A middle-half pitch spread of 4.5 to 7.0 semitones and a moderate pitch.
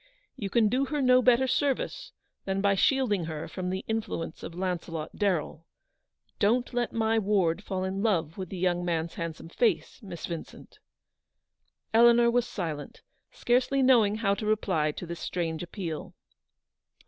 No: wide, 5.6 semitones; high, 195 Hz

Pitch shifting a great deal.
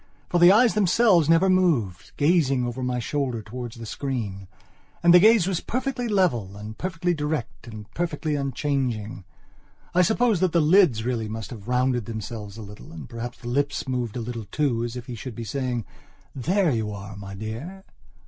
Yes: wide, 7.4 semitones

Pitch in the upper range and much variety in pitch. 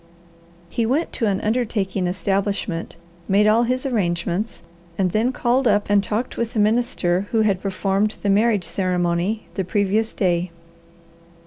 No: high, 205 Hz; average, 3.1 semitones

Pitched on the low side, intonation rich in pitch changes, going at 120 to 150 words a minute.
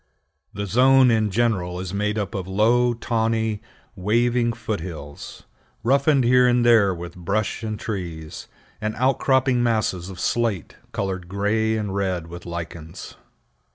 No: low, 105 Hz; average, 4.3 semitones; average, 140 wpm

